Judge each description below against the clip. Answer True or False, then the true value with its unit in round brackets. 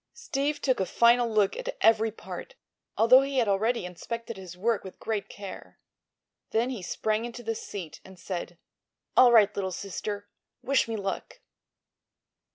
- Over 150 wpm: True (160 wpm)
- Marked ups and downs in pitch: False (3.6 semitones)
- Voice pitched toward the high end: True (220 Hz)